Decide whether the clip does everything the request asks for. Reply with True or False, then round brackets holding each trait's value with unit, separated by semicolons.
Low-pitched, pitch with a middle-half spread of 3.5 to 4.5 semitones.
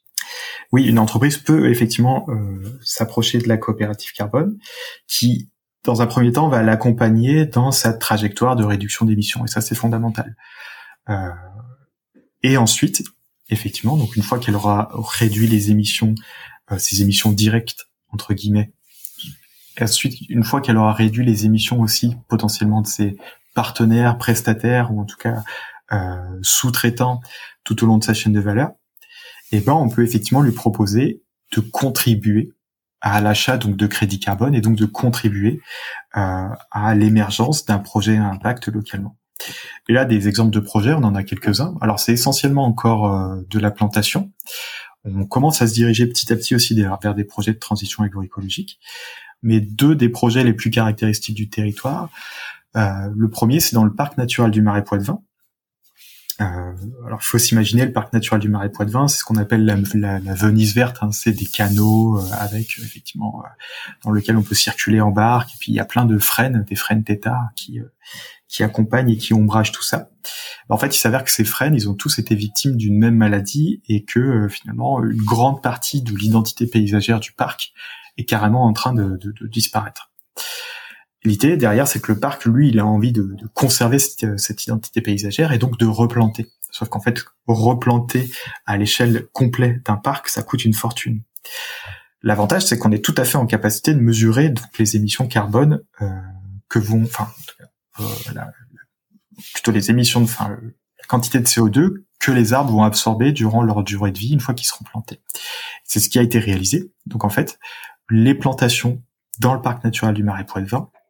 False (115 Hz; 2.7 semitones)